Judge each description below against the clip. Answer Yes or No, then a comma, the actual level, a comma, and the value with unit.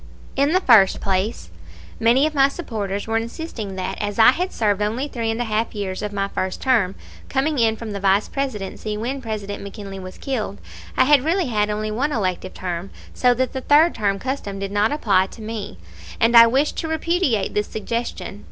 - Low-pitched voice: No, high, 220 Hz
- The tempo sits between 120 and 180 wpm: No, average, 200 wpm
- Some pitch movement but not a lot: Yes, average, 4.8 semitones